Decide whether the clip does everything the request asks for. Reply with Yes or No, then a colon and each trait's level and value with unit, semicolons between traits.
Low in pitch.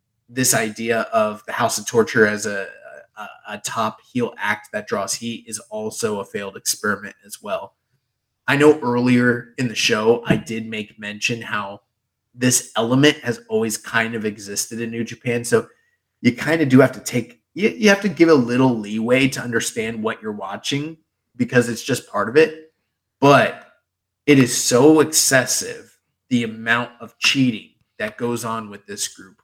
Yes: low, 120 Hz